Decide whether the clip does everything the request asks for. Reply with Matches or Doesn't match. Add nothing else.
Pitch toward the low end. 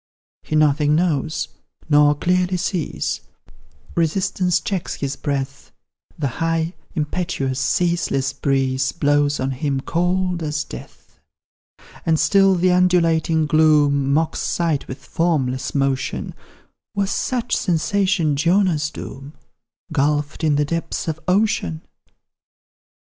Doesn't match